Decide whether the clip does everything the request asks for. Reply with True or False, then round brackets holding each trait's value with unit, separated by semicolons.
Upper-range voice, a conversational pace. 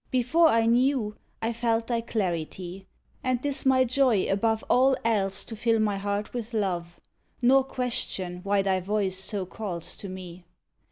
True (220 Hz; 160 wpm)